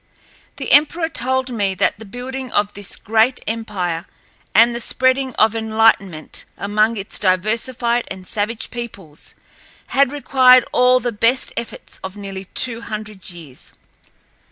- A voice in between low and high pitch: No, high, 225 Hz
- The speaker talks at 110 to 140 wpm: Yes, slow, 135 wpm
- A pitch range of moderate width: Yes, average, 3.9 semitones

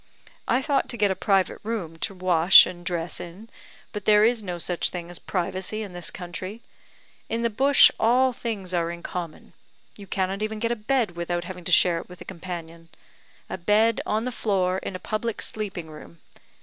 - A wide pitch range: No, average, 3.8 semitones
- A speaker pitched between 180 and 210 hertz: Yes, high, 190 Hz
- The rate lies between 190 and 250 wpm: Yes, average, 200 wpm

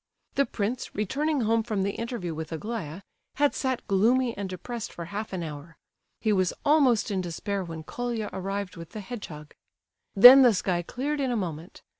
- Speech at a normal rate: Yes, average, 180 wpm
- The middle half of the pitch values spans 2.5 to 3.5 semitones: No, average, 5.3 semitones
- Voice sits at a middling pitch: No, high, 205 Hz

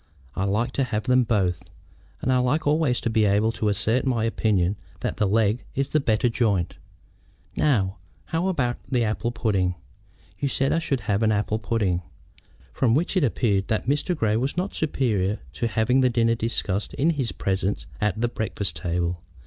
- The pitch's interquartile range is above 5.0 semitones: No, average, 4.0 semitones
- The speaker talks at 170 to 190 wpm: Yes, average, 185 wpm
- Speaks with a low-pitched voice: Yes, low, 115 Hz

